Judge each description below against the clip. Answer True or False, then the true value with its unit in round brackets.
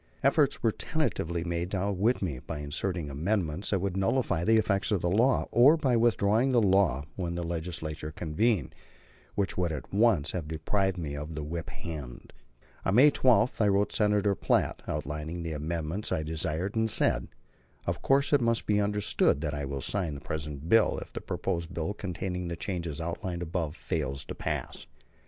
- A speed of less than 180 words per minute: False (185 wpm)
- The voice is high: False (90 Hz)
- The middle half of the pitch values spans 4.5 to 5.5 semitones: True (4.8 semitones)